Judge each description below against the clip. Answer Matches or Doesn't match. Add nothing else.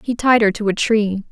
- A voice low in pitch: Doesn't match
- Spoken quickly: Matches